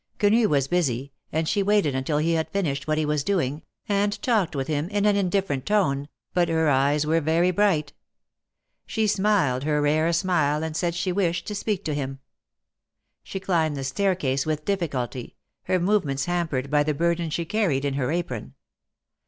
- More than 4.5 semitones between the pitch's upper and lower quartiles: Yes, average, 4.9 semitones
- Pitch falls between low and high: Yes, medium, 160 Hz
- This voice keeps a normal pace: Yes, average, 180 wpm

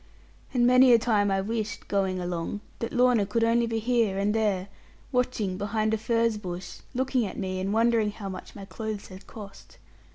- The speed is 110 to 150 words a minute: No, average, 190 wpm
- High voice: Yes, high, 215 Hz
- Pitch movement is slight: No, average, 3.0 semitones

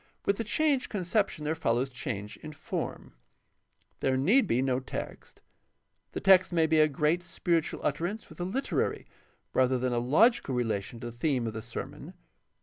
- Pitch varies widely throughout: Yes, wide, 6.4 semitones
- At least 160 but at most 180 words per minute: Yes, average, 170 wpm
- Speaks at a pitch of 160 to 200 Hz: No, medium, 150 Hz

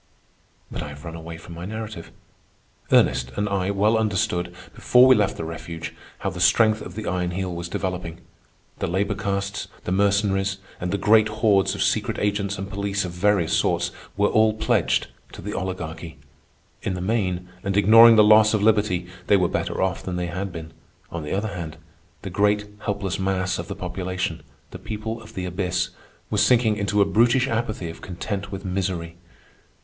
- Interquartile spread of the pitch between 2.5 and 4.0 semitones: Yes, average, 2.8 semitones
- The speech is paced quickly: No, average, 185 wpm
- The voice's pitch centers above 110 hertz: No, very low, 95 Hz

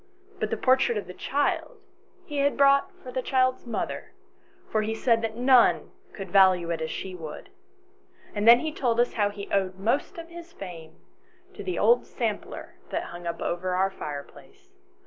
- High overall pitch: Yes, high, 225 Hz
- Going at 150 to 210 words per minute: Yes, average, 180 wpm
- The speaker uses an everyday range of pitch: No, wide, 6.4 semitones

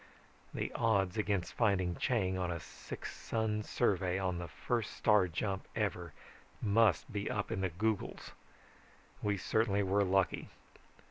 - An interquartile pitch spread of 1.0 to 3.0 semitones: Yes, narrow, 2.5 semitones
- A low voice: Yes, low, 100 Hz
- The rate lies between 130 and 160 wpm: Yes, average, 140 wpm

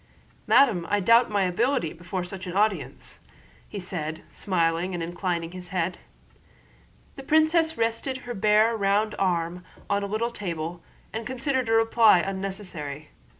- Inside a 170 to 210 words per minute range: No, average, 140 wpm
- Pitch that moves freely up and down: No, average, 4.4 semitones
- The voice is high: Yes, high, 195 Hz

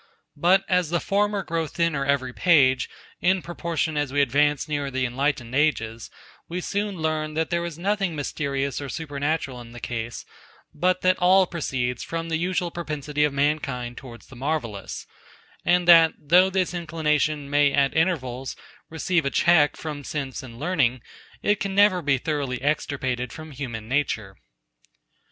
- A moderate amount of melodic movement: Yes, average, 4.2 semitones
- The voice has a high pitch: No, medium, 150 Hz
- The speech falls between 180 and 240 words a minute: No, average, 160 wpm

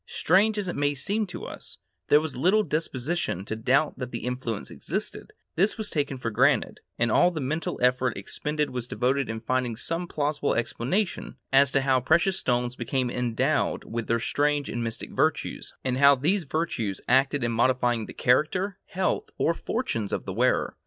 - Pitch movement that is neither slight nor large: Yes, average, 4.7 semitones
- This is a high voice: No, low, 135 Hz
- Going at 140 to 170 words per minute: No, average, 180 wpm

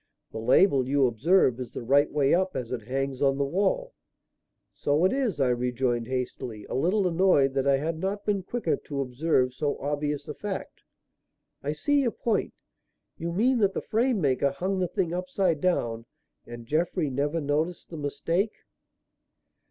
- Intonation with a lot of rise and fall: Yes, wide, 5.9 semitones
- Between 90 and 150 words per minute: No, average, 175 wpm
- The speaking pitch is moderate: Yes, medium, 150 Hz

